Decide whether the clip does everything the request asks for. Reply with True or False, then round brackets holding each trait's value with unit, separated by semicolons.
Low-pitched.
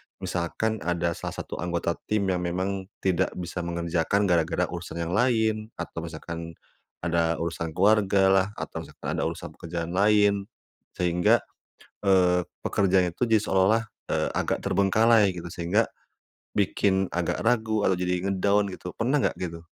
True (90 Hz)